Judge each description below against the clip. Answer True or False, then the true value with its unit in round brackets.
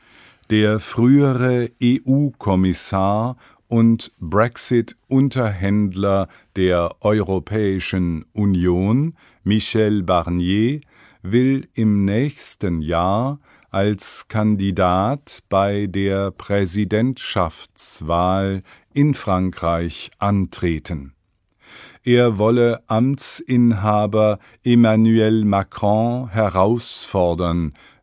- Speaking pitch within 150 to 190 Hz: False (105 Hz)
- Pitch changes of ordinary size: True (3.9 semitones)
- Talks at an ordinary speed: False (60 wpm)